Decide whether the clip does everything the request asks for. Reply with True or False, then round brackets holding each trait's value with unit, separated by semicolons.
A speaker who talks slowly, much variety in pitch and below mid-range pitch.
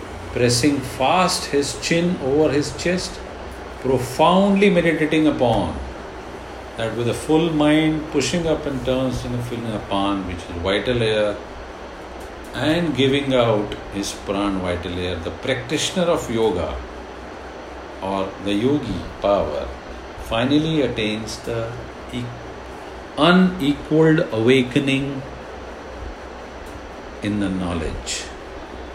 True (105 wpm; 7.3 semitones; 125 Hz)